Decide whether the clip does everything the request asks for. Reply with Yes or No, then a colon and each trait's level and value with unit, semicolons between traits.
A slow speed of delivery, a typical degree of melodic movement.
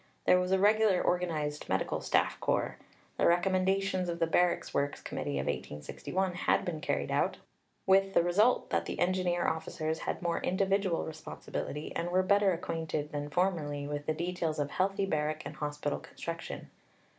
No: average, 165 wpm; average, 3.4 semitones